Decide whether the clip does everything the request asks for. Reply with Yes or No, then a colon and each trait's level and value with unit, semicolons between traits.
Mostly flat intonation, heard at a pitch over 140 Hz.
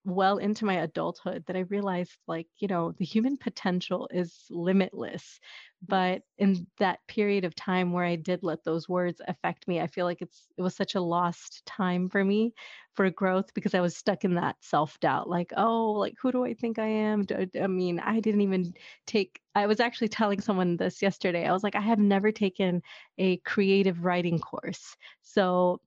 Yes: narrow, 2.3 semitones; medium, 185 Hz